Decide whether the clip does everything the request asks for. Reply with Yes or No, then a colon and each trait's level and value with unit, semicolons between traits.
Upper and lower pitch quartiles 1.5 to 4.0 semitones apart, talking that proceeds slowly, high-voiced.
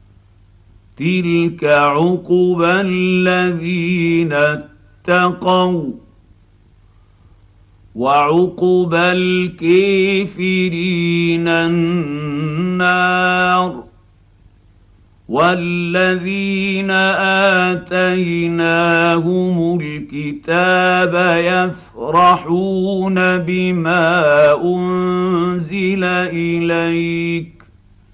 No: average, 3.6 semitones; slow, 30 wpm; medium, 175 Hz